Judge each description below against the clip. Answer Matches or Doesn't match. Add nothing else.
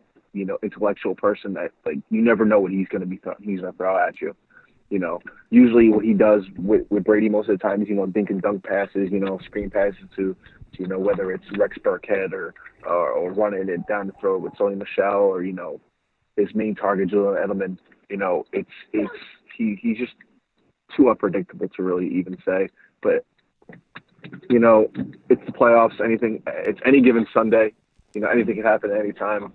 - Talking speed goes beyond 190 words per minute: Matches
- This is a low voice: Matches